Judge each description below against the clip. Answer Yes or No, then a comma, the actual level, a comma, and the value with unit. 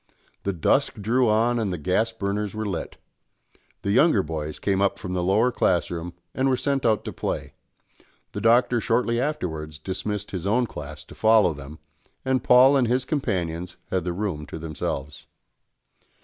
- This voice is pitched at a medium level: No, low, 100 Hz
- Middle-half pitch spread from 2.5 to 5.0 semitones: No, wide, 5.6 semitones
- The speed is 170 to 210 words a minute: Yes, average, 175 wpm